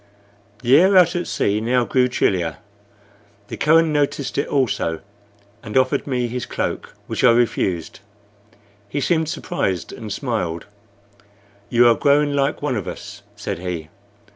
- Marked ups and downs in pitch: Yes, wide, 5.7 semitones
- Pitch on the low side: Yes, low, 125 Hz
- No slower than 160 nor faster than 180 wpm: No, average, 145 wpm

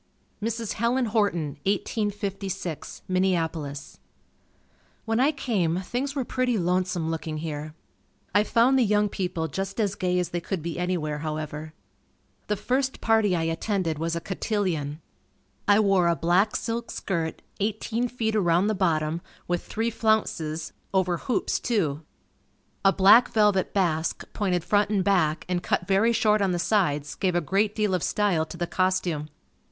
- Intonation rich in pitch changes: No, average, 4.2 semitones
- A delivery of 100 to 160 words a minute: Yes, average, 155 wpm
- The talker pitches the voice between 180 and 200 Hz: Yes, high, 190 Hz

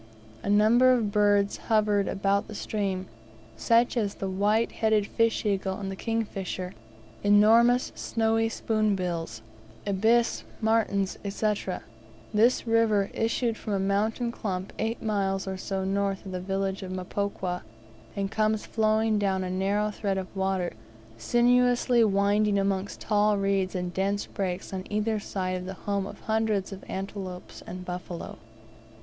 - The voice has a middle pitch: No, high, 200 Hz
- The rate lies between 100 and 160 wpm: Yes, average, 140 wpm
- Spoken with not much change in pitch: Yes, narrow, 2.3 semitones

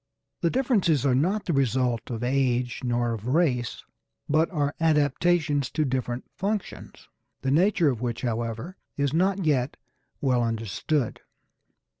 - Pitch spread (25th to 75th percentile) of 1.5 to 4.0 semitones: No, average, 5.1 semitones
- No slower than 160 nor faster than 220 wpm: No, slow, 135 wpm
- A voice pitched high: No, low, 135 Hz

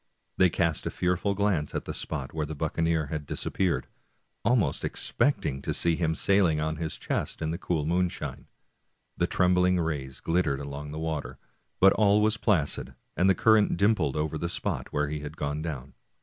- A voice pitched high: No, very low, 80 Hz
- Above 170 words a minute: Yes, average, 180 wpm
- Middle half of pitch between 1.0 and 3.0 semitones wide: No, average, 3.4 semitones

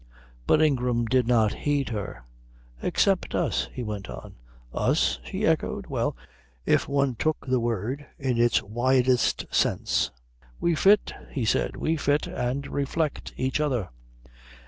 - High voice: No, low, 125 Hz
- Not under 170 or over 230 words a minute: No, average, 140 wpm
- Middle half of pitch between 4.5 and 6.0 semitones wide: No, average, 3.6 semitones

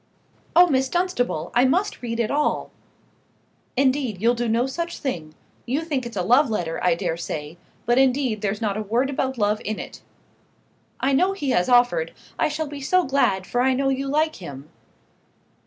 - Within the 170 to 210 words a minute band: Yes, average, 190 wpm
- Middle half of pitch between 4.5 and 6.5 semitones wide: Yes, average, 5.0 semitones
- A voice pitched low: No, very high, 250 Hz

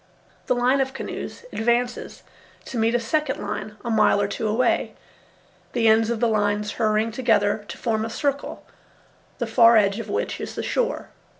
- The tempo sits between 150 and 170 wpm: No, average, 180 wpm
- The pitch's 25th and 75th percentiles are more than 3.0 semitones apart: No, narrow, 2.4 semitones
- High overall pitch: Yes, high, 230 Hz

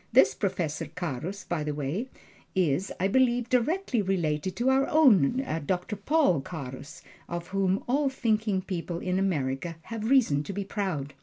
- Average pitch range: No, wide, 6.5 semitones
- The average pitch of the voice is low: No, high, 190 Hz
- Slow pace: No, average, 155 wpm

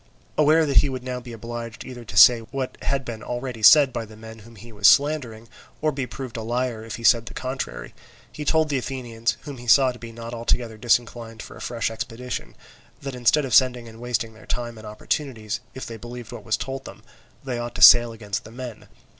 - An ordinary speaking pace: No, fast, 225 wpm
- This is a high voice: No, low, 120 Hz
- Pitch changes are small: Yes, narrow, 2.3 semitones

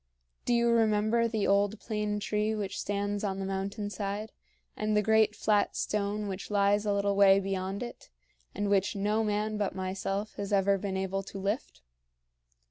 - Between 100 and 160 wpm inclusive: No, average, 175 wpm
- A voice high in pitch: Yes, high, 205 Hz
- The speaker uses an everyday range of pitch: No, narrow, 1.4 semitones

